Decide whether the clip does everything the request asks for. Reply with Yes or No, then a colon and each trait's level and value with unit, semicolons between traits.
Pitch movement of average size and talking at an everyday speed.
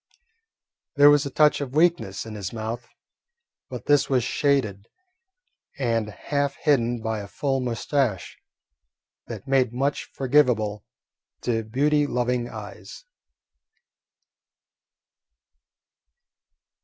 No: average, 4.1 semitones; slow, 100 wpm